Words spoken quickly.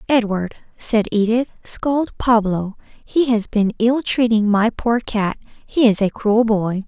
No: average, 155 wpm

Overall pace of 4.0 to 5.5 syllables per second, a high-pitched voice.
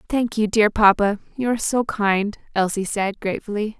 Yes: 5.2 syllables/s; high, 210 Hz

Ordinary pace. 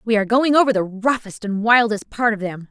No: fast, 245 wpm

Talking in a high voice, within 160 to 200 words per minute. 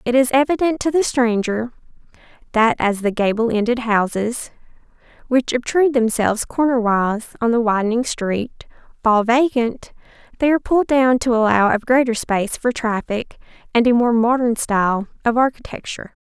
No: high, 235 Hz; average, 150 wpm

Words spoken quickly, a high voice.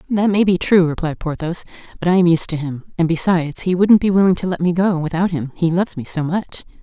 No: fast, 255 wpm; medium, 175 Hz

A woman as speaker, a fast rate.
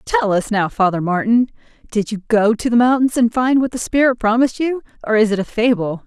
Yes: female; fast, 230 wpm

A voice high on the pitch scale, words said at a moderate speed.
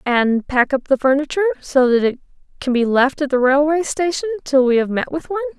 No: very high, 280 Hz; fast, 225 wpm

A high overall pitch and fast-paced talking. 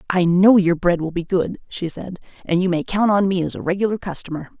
No: medium, 180 Hz; fast, 250 wpm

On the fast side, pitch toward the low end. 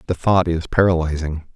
No: average, 155 wpm; very low, 85 Hz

